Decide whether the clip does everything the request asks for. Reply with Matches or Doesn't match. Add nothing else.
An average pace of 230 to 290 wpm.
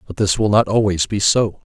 Matches